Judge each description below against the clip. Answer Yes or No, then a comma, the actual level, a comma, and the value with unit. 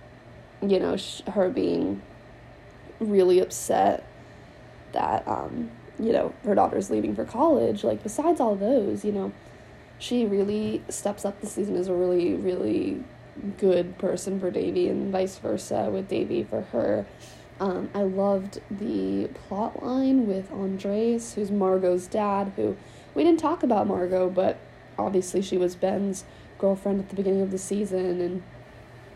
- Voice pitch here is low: No, high, 195 Hz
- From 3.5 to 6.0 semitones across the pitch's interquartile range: No, narrow, 2.4 semitones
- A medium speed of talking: Yes, average, 150 wpm